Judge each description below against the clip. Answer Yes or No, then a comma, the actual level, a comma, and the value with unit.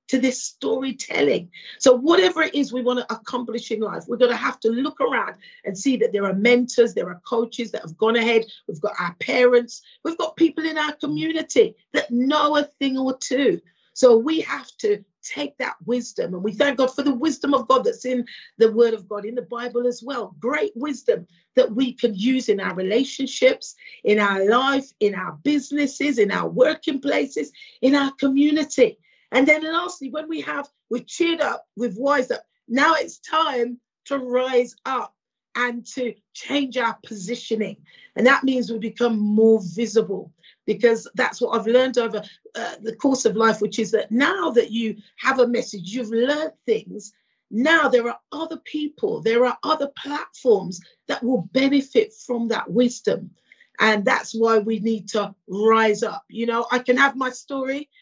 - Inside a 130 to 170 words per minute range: No, average, 185 wpm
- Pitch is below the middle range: No, very high, 250 Hz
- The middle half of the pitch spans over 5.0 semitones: No, average, 4.2 semitones